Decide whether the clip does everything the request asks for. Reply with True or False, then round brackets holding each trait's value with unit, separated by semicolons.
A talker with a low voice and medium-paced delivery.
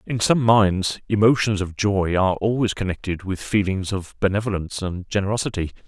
True (100 Hz; 155 wpm)